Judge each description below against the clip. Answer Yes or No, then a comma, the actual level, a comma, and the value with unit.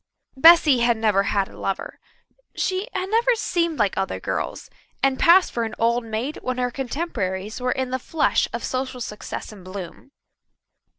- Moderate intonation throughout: No, wide, 6.9 semitones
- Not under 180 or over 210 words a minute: No, average, 170 wpm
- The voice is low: No, very high, 250 Hz